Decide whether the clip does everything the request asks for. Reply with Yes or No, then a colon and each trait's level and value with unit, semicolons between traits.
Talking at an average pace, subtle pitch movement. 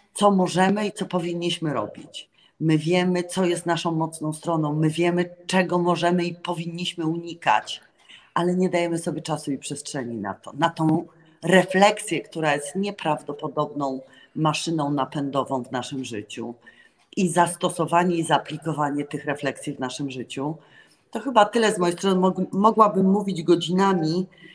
No: average, 140 wpm; average, 3.4 semitones